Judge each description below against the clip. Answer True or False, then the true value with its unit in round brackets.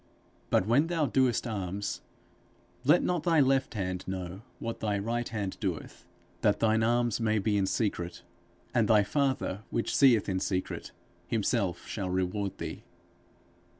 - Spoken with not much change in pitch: False (3.9 semitones)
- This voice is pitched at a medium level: False (110 Hz)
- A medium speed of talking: True (150 wpm)